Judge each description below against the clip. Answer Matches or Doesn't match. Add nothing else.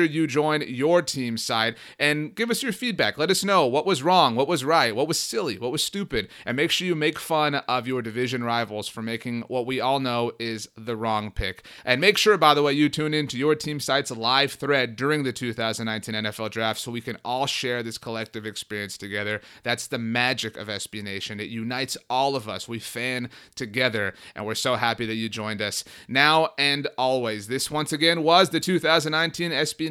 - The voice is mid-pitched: Doesn't match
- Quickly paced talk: Matches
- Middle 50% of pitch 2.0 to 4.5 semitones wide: Doesn't match